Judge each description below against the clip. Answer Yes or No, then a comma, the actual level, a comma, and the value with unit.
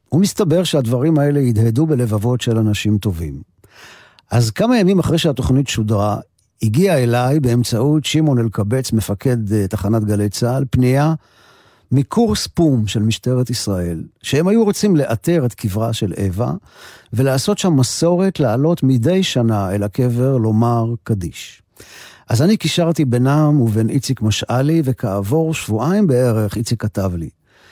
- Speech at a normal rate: Yes, average, 130 wpm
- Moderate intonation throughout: No, wide, 5.8 semitones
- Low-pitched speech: Yes, low, 125 Hz